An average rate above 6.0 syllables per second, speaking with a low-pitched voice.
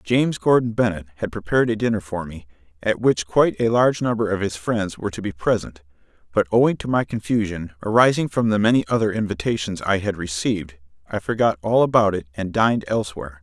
Yes: 6.2 syllables/s; low, 100 Hz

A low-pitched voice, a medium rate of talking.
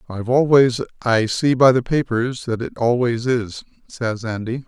Yes: low, 120 Hz; average, 155 wpm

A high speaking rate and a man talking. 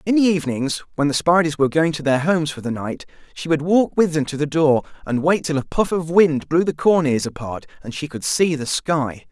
Yes: fast, 260 wpm; male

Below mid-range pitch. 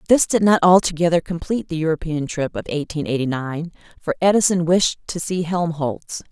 No: medium, 165 Hz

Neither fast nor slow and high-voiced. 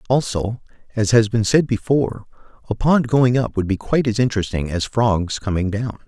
No: average, 190 wpm; low, 115 Hz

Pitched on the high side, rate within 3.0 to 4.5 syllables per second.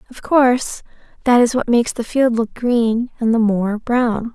Yes: high, 235 Hz; 4.4 syllables/s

